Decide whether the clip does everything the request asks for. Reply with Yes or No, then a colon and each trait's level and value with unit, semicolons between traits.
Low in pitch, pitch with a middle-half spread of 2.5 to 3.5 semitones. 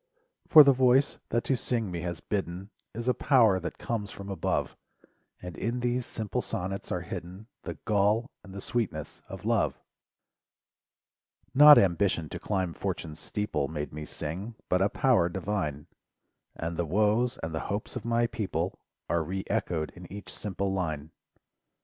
No: low, 100 Hz; average, 5.2 semitones